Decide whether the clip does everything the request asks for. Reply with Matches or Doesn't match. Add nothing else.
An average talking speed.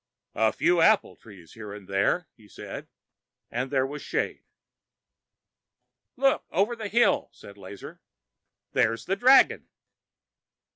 Doesn't match